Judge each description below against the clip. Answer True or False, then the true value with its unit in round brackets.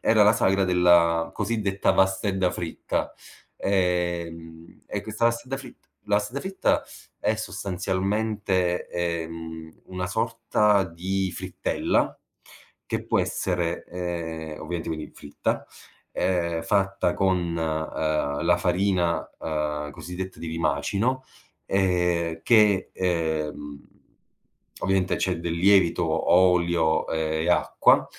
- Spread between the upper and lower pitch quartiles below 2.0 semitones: False (2.8 semitones)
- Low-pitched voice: True (90 Hz)